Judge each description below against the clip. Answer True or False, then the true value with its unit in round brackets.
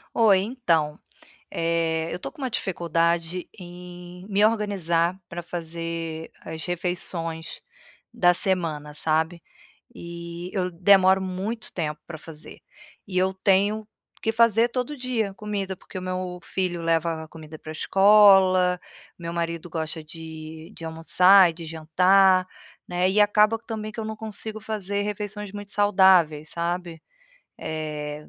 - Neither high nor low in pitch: True (180 Hz)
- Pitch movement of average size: True (3.5 semitones)